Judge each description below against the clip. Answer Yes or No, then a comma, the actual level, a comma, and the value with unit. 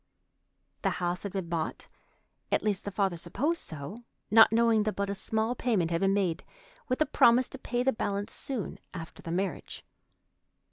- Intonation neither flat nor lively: Yes, average, 4.5 semitones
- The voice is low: No, high, 200 Hz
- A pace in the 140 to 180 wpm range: Yes, average, 170 wpm